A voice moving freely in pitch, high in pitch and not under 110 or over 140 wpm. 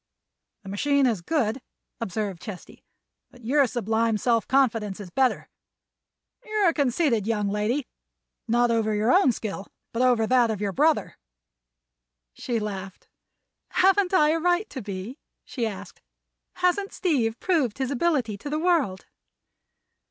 Yes: wide, 5.9 semitones; high, 240 Hz; slow, 135 wpm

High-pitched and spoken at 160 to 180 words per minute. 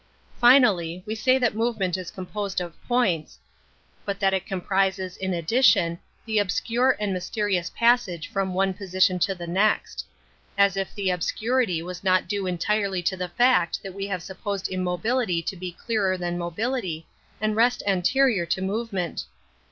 Yes: high, 195 Hz; average, 165 wpm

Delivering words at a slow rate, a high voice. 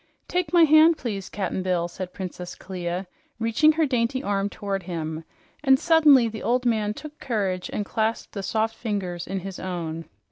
No: average, 175 wpm; high, 205 Hz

